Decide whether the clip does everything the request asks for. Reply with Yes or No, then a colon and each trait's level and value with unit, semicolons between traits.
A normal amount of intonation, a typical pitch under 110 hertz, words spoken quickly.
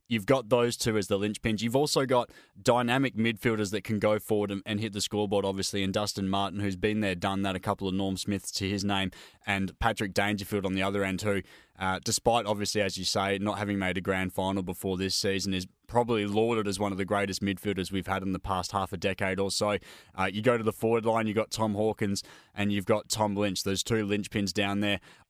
No: narrow, 1.9 semitones; low, 100 Hz; fast, 240 wpm